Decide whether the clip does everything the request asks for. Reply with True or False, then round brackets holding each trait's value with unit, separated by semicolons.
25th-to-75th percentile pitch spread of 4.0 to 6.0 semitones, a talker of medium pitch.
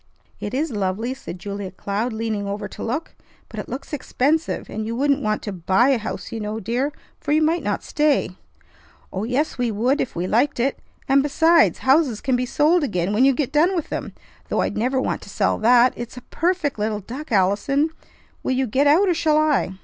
False (5.6 semitones; 250 Hz)